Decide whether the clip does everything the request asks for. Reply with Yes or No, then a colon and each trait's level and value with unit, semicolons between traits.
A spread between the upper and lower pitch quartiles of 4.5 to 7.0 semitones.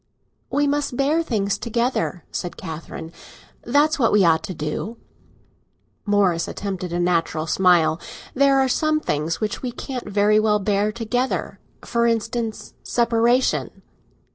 Yes: wide, 5.6 semitones